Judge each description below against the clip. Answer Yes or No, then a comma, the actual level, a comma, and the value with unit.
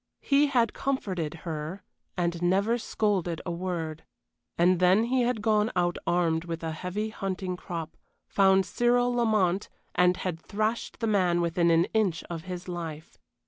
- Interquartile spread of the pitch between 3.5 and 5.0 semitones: Yes, average, 3.9 semitones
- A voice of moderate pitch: Yes, medium, 180 Hz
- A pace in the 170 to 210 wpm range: No, average, 155 wpm